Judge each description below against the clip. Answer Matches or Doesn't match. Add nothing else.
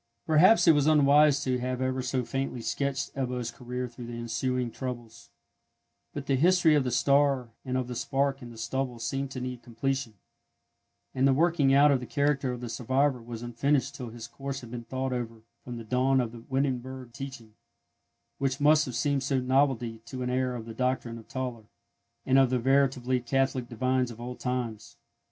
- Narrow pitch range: Matches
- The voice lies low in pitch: Matches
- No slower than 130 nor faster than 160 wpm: Doesn't match